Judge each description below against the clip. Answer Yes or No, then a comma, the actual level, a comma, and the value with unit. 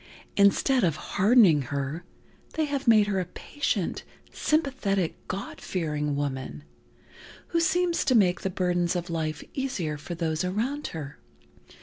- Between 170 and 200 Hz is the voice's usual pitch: Yes, medium, 185 Hz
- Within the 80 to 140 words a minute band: Yes, slow, 135 wpm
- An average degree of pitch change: No, wide, 7.7 semitones